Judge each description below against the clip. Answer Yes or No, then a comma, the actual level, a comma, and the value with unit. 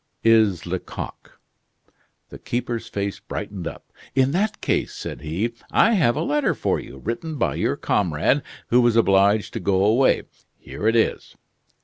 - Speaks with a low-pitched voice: Yes, low, 115 Hz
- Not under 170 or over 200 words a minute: No, average, 155 wpm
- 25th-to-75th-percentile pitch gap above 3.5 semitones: Yes, average, 4.1 semitones